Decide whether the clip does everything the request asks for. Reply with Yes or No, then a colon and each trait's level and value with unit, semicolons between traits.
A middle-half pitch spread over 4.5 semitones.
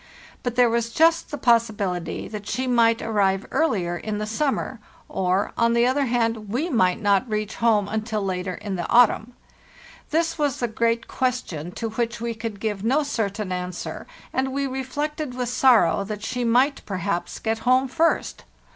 No: average, 3.7 semitones